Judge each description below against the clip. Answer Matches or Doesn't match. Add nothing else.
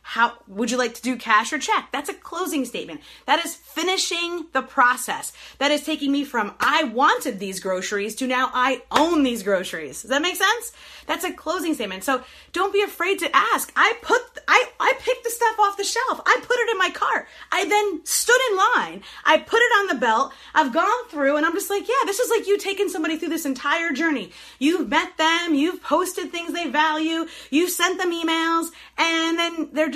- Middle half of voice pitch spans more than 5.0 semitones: Matches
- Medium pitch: Doesn't match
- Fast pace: Matches